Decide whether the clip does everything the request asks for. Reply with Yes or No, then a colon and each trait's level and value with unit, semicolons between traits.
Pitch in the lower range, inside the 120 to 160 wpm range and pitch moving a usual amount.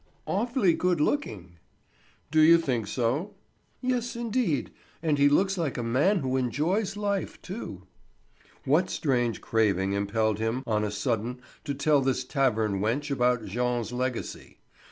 No: low, 130 Hz; average, 140 wpm; wide, 7.1 semitones